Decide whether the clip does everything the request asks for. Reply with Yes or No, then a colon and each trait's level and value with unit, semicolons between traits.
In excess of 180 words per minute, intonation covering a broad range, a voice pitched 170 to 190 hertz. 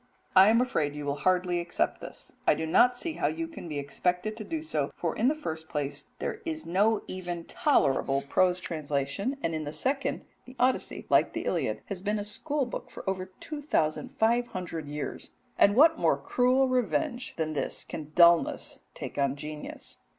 Yes: average, 195 wpm; wide, 8.5 semitones; medium, 185 Hz